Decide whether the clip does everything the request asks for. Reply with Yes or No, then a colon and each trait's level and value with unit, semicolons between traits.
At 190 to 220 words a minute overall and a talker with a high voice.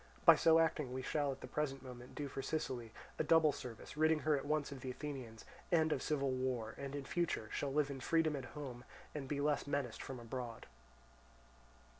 No: fast, 205 wpm; medium, 140 Hz